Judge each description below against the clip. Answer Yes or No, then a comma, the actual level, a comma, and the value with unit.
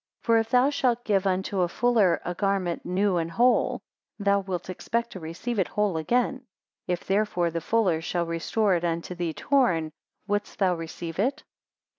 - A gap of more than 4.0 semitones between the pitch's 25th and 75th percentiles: Yes, average, 4.7 semitones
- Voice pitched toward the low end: No, high, 190 Hz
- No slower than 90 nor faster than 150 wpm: No, average, 175 wpm